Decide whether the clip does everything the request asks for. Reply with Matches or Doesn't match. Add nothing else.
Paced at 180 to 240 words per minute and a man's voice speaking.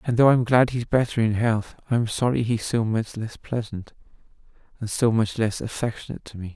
Matches